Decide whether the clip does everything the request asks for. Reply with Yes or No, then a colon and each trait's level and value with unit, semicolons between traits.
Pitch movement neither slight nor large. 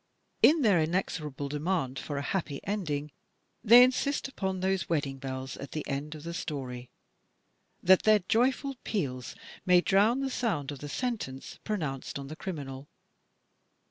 No: wide, 6.9 semitones